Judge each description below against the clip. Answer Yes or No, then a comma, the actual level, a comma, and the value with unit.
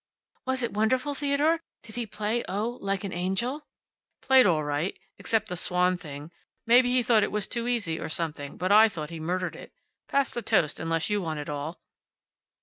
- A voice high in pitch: Yes, high, 205 Hz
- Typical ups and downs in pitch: No, wide, 6.4 semitones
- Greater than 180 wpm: Yes, average, 195 wpm